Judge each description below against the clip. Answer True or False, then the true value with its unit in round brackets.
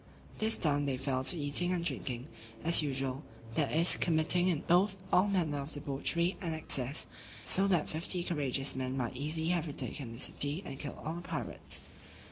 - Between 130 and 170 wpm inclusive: False (180 wpm)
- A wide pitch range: False (4.1 semitones)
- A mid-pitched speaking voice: True (155 Hz)